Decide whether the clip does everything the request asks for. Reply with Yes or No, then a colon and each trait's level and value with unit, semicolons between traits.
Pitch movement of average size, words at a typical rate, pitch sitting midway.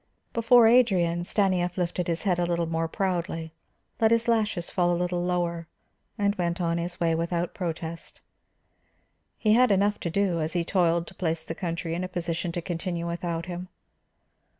No: narrow, 2.1 semitones; average, 175 wpm; medium, 175 Hz